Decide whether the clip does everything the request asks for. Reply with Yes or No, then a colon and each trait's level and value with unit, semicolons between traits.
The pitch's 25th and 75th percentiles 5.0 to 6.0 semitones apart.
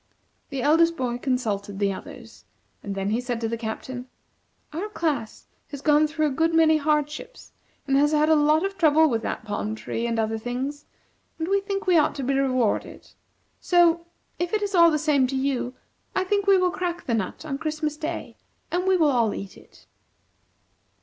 Yes: wide, 5.4 semitones